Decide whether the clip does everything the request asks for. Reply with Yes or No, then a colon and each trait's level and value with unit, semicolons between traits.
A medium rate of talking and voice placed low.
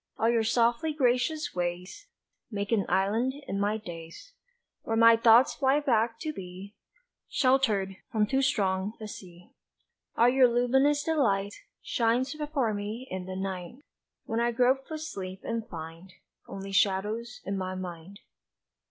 No: average, 145 wpm; high, 225 Hz